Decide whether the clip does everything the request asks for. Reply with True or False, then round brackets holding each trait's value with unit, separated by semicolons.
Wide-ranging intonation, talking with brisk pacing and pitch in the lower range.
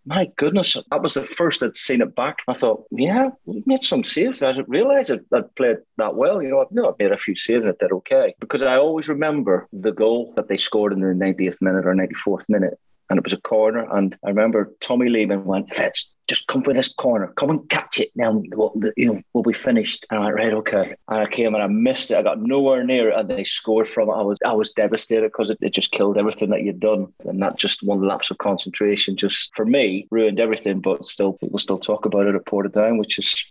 True (6.6 semitones; 255 wpm; 110 Hz)